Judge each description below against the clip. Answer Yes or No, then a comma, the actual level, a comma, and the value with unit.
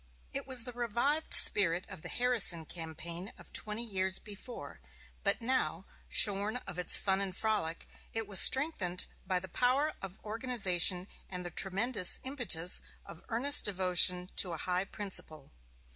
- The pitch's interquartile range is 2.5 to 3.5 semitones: No, average, 4.7 semitones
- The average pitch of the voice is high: Yes, high, 195 Hz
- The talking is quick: No, average, 150 wpm